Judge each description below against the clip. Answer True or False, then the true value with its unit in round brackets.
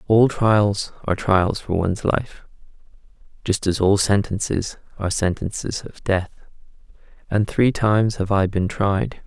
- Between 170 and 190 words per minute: False (140 wpm)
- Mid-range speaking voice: False (100 Hz)